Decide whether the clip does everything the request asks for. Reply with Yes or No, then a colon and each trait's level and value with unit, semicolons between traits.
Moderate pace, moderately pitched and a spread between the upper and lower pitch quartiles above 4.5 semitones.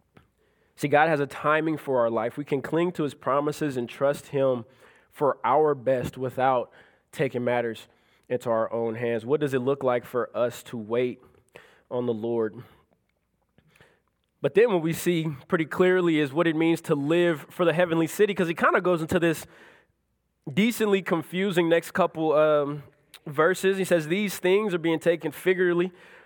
Yes: average, 175 wpm; medium, 155 Hz; average, 5.2 semitones